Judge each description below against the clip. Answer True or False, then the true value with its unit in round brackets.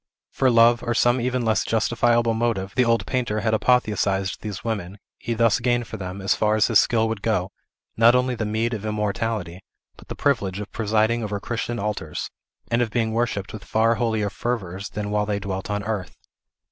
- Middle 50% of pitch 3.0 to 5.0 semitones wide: False (2.4 semitones)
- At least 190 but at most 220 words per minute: True (195 wpm)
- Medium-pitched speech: False (110 Hz)